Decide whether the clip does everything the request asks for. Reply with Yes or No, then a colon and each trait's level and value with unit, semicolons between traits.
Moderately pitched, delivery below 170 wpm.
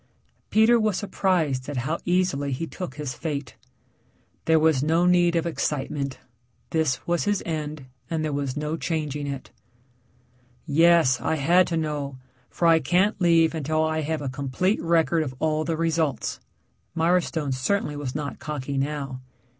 Yes: medium, 155 Hz; average, 155 wpm